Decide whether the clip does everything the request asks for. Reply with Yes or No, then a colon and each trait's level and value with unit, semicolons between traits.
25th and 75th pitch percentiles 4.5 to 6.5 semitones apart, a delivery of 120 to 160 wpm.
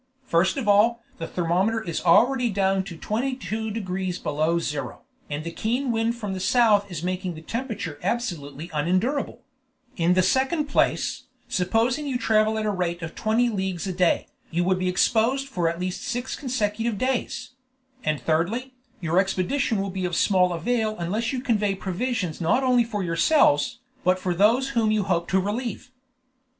No: average, 5.0 semitones; average, 170 wpm